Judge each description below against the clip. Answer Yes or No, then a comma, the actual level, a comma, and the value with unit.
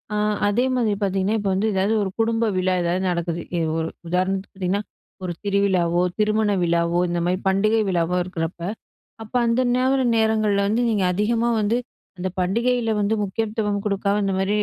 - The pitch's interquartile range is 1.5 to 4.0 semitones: Yes, average, 3.2 semitones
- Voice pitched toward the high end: Yes, high, 200 Hz